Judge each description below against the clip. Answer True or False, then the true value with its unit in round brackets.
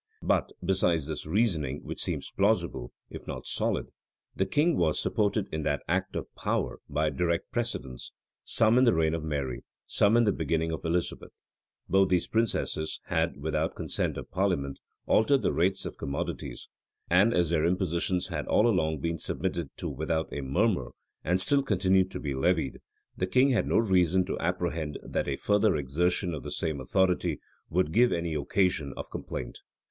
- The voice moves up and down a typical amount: True (3.7 semitones)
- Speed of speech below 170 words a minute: False (175 wpm)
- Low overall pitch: True (85 Hz)